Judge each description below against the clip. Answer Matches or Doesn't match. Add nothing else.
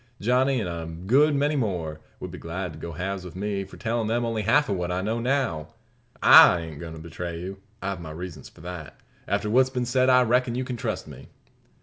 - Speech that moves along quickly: Matches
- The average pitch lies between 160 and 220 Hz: Doesn't match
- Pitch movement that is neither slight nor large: Doesn't match